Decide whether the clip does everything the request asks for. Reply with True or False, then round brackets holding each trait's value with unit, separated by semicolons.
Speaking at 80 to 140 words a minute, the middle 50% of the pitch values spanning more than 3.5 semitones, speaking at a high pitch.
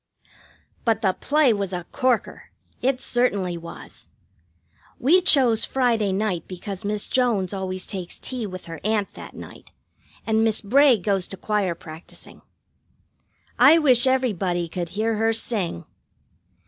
True (135 wpm; 4.7 semitones; 210 Hz)